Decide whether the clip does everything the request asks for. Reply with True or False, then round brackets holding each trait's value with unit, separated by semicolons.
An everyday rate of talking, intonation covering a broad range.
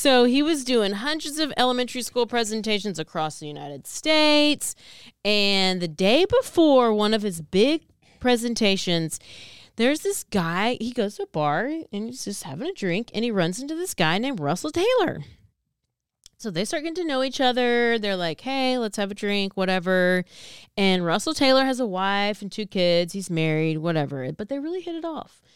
True (185 wpm; 6.2 semitones)